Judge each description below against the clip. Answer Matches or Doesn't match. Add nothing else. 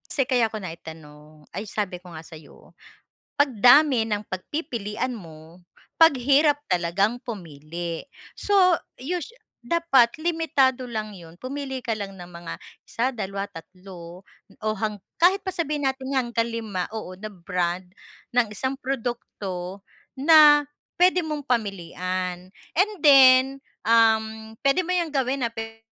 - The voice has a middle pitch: Doesn't match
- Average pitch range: Doesn't match